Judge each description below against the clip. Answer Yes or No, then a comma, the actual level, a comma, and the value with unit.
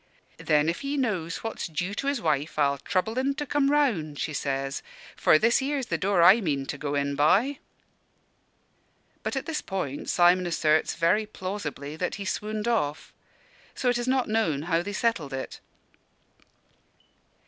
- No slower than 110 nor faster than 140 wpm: No, average, 170 wpm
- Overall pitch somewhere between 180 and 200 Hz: Yes, medium, 185 Hz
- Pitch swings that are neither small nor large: No, wide, 7.7 semitones